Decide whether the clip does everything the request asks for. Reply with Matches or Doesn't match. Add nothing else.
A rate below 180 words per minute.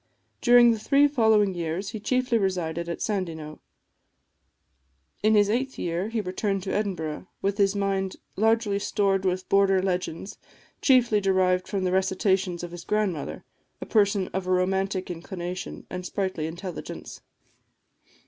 Matches